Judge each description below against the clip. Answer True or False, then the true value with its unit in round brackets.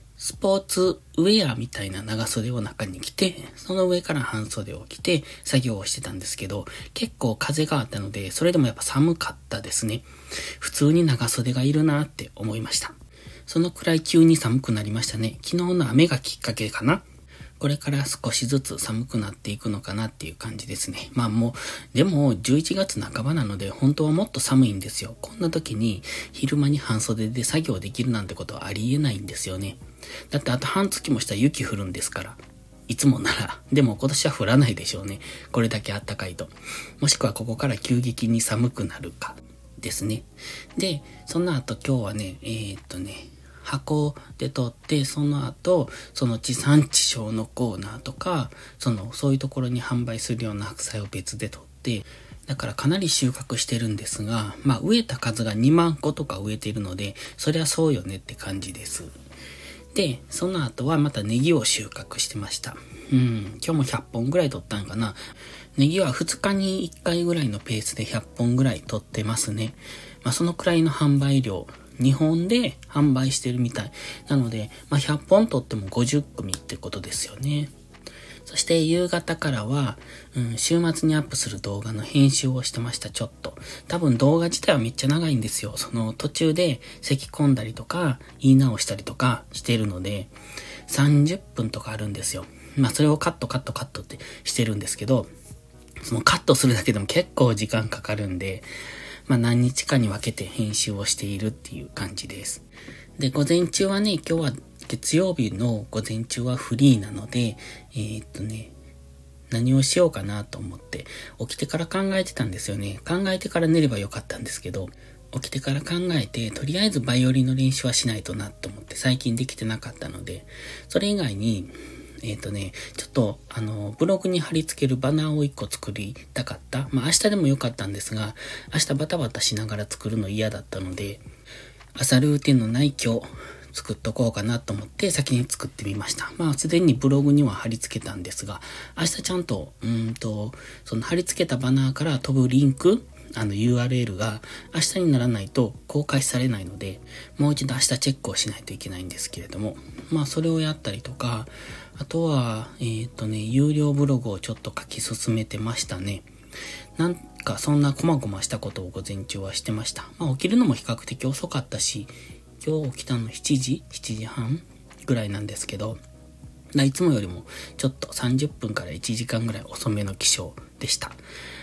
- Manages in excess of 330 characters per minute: True (360 characters per minute)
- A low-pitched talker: True (125 Hz)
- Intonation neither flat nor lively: True (4.8 semitones)